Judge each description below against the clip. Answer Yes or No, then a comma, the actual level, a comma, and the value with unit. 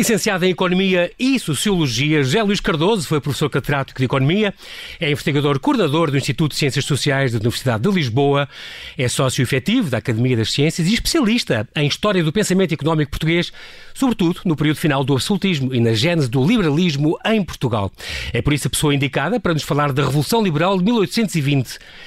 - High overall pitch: No, medium, 155 Hz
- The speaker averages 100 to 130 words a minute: No, average, 180 wpm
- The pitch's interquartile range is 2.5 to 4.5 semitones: No, average, 5.1 semitones